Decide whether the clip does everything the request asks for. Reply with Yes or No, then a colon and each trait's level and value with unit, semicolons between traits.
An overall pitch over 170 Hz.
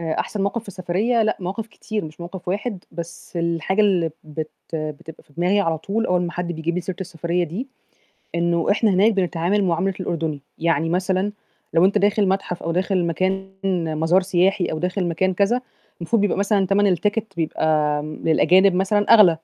Yes: medium, 185 Hz